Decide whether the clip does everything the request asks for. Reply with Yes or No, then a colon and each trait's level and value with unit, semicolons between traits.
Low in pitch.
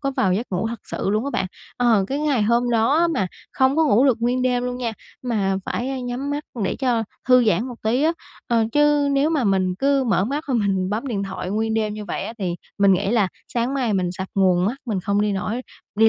No: high, 230 Hz